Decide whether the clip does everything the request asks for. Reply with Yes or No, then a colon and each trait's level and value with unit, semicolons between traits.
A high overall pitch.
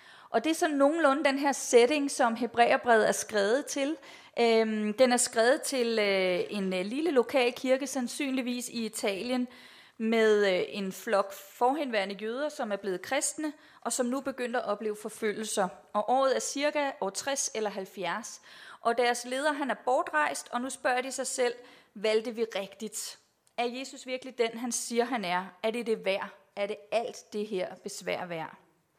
Yes: high, 240 Hz